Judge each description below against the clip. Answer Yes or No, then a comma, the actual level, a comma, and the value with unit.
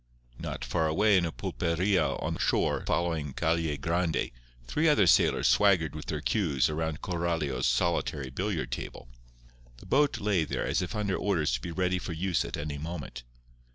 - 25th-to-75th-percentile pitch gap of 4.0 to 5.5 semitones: No, average, 3.5 semitones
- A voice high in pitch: No, very low, 85 Hz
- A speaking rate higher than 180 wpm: No, average, 175 wpm